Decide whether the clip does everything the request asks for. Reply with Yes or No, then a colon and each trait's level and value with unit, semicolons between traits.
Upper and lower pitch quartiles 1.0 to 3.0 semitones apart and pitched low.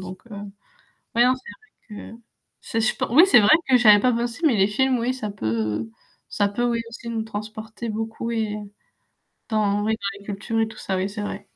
No: average, 2.7 semitones; high, 220 Hz